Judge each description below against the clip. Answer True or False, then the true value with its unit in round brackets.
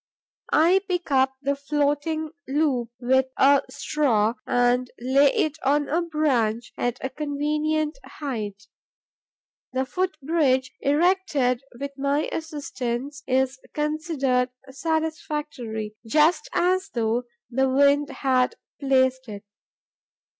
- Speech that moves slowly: True (110 wpm)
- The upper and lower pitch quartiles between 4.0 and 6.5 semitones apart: False (3.2 semitones)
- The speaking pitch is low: False (280 Hz)